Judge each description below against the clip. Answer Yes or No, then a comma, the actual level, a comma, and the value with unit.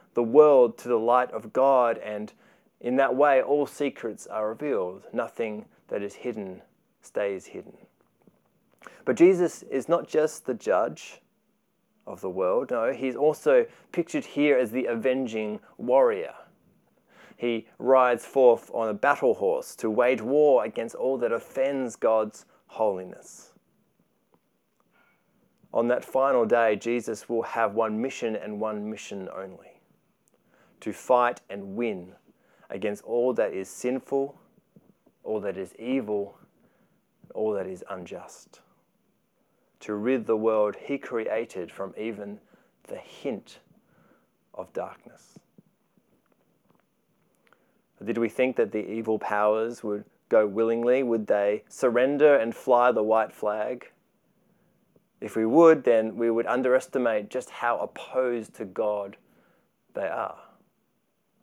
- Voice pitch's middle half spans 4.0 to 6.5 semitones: Yes, average, 4.5 semitones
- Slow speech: Yes, slow, 125 wpm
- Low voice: Yes, low, 120 Hz